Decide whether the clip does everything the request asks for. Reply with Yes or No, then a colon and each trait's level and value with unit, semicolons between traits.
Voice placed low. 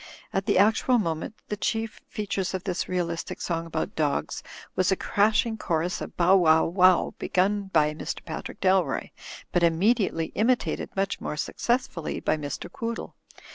No: medium, 185 Hz